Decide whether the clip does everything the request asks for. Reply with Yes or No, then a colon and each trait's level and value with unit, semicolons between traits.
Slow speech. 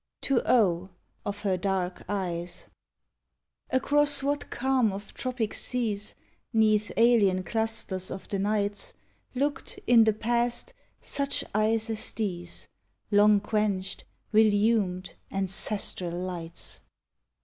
Yes: slow, 105 wpm